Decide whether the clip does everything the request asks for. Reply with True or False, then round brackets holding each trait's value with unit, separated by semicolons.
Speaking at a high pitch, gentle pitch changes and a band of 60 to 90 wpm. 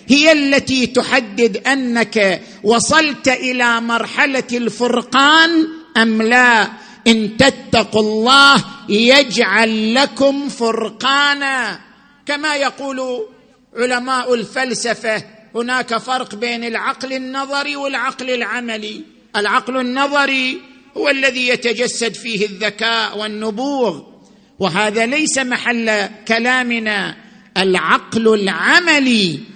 False (245 Hz; 3.2 semitones; 85 wpm)